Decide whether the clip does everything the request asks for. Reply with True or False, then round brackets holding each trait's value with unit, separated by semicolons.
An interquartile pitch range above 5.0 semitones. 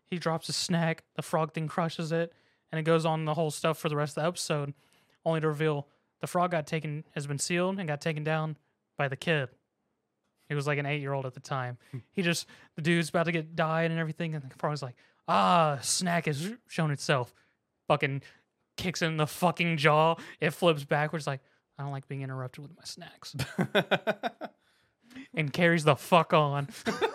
False (2.6 semitones)